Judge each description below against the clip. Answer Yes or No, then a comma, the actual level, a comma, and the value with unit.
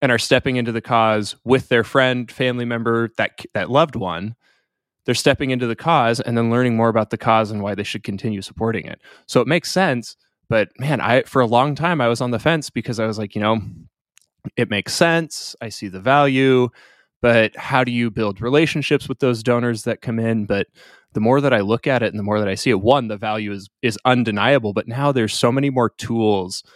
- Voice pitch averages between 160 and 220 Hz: No, low, 120 Hz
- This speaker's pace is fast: Yes, fast, 230 wpm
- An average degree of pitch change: Yes, average, 3.0 semitones